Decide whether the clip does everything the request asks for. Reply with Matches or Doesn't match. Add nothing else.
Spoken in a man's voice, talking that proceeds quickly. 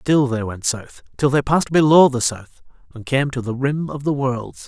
Matches